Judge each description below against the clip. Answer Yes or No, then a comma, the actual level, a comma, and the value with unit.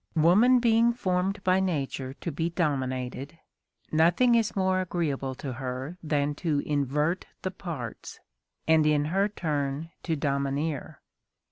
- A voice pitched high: No, medium, 160 Hz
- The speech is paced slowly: Yes, slow, 130 wpm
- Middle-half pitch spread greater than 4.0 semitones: Yes, average, 5.0 semitones